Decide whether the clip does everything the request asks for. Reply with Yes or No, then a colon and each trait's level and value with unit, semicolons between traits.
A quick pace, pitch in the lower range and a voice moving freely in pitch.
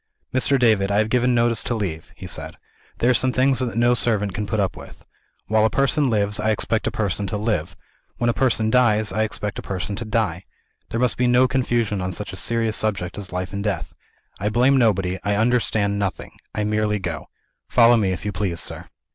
No: fast, 220 wpm; low, 110 Hz; average, 2.9 semitones